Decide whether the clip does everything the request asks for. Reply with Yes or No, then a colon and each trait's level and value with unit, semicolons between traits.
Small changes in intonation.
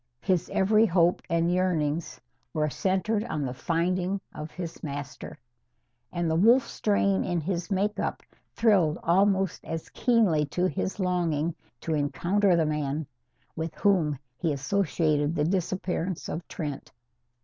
No: average, 3.7 semitones